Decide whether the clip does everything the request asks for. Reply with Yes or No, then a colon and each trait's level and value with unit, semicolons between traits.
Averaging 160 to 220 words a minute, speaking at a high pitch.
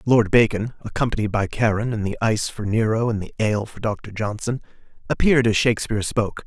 No: average, 185 wpm; low, 110 Hz